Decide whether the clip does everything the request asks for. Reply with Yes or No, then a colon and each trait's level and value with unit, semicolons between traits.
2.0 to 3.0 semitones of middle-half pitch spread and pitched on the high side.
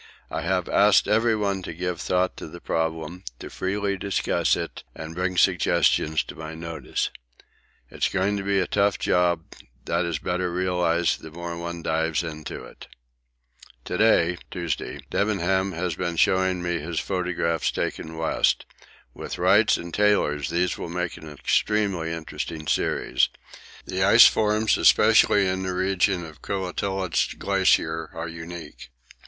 No: narrow, 2.6 semitones; very low, 90 Hz